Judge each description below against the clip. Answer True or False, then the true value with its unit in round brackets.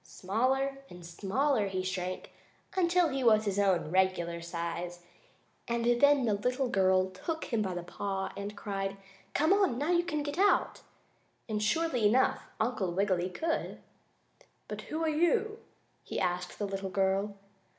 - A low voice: False (205 Hz)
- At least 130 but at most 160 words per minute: True (155 wpm)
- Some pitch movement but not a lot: False (6.7 semitones)